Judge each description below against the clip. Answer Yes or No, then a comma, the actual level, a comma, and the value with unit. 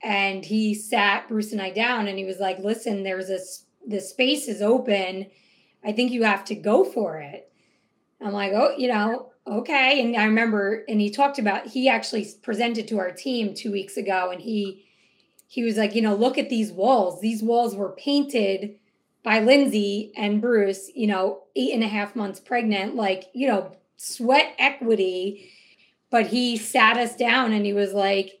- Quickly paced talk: No, average, 190 wpm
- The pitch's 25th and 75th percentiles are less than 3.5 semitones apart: Yes, average, 3.1 semitones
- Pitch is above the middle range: Yes, high, 215 Hz